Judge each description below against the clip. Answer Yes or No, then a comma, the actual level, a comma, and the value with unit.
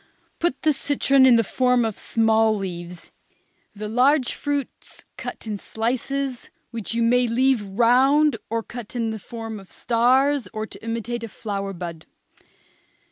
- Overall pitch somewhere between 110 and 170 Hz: No, high, 230 Hz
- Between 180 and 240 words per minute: No, average, 150 wpm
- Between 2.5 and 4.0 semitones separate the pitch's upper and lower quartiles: Yes, average, 3.1 semitones